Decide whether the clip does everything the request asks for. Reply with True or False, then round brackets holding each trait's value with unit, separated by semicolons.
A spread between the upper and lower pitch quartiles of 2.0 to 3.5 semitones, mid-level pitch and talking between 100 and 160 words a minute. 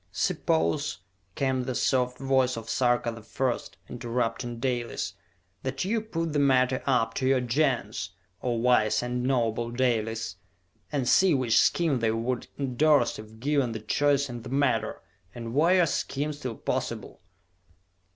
False (2.8 semitones; 125 Hz; 150 wpm)